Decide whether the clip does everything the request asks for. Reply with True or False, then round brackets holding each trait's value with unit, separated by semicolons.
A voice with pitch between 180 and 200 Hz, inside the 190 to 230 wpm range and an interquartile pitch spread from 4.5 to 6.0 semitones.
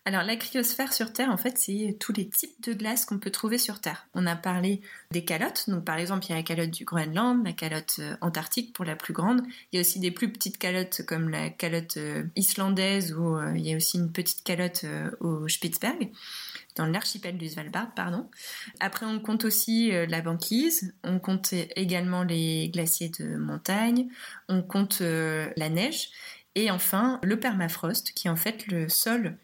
True (185 Hz; 205 wpm; 4.9 semitones)